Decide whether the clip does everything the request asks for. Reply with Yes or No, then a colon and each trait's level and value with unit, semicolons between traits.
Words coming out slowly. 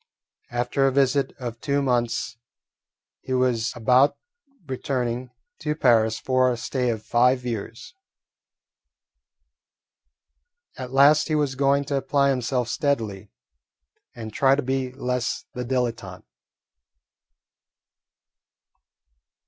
Yes: slow, 105 wpm